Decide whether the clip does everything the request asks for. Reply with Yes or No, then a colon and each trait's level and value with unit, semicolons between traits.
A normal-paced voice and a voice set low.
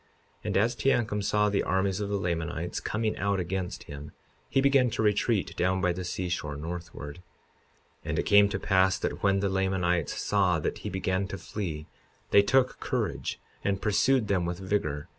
Yes: average, 180 wpm; very low, 95 Hz